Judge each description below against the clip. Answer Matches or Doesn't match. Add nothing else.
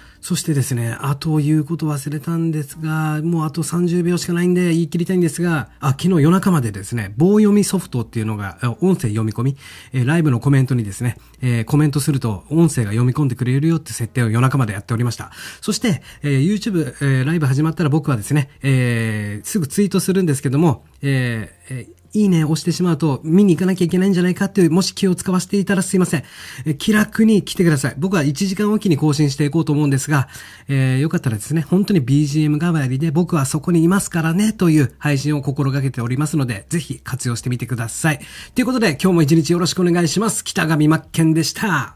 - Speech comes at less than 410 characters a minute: Doesn't match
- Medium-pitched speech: Matches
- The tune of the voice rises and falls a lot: Doesn't match